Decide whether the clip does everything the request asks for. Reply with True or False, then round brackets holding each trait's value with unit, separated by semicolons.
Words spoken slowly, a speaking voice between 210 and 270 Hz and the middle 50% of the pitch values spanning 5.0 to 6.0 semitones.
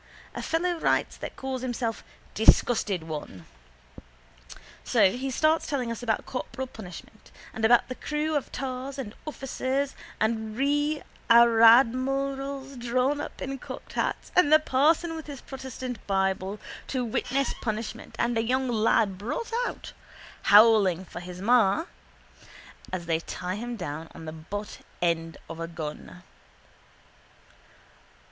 True (130 wpm; 240 Hz; 5.4 semitones)